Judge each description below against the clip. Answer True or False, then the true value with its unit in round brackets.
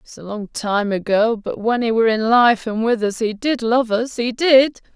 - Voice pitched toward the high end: True (230 Hz)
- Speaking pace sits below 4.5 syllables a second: False (4.7 syllables/s)